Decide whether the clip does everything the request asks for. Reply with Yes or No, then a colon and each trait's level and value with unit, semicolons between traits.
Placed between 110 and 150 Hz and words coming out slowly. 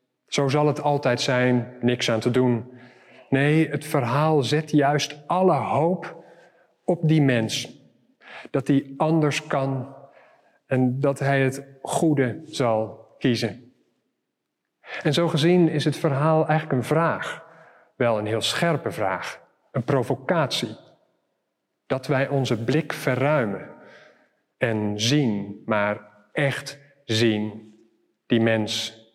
Yes: low, 135 Hz; slow, 120 wpm